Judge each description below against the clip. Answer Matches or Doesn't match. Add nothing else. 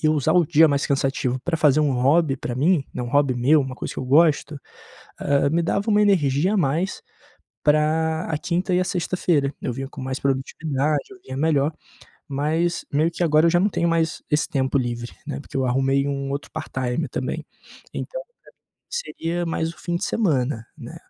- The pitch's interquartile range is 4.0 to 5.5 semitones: Doesn't match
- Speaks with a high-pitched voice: Doesn't match